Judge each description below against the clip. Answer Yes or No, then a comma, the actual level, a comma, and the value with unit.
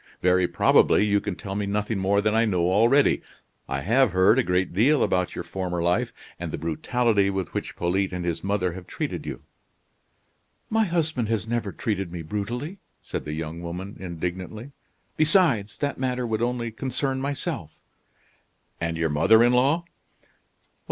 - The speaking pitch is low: Yes, low, 100 Hz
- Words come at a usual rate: Yes, average, 165 wpm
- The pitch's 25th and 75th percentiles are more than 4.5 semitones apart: Yes, average, 5.3 semitones